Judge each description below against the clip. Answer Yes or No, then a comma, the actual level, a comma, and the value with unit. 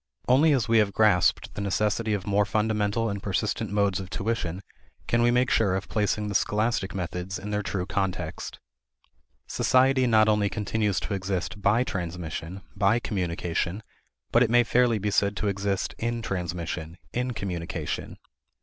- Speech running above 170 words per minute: No, average, 160 wpm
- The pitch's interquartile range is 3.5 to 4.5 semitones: No, average, 2.8 semitones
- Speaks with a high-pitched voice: No, low, 100 Hz